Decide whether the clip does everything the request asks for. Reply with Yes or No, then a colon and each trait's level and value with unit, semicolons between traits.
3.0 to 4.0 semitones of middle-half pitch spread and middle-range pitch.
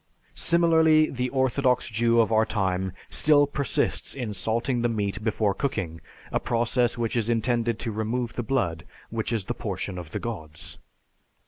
No: average, 3.4 semitones; low, 115 Hz